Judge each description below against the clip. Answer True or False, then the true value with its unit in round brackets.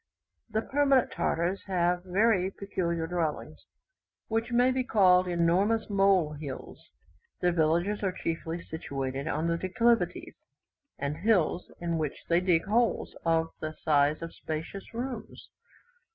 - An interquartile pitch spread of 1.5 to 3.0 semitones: False (4.2 semitones)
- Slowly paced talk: True (125 wpm)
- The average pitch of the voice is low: False (180 Hz)